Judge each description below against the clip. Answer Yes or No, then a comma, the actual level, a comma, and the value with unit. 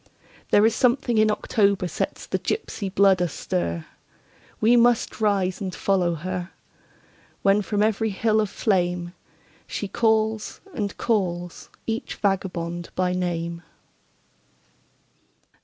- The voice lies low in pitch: No, high, 195 Hz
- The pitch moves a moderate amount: Yes, average, 3.5 semitones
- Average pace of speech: No, slow, 105 wpm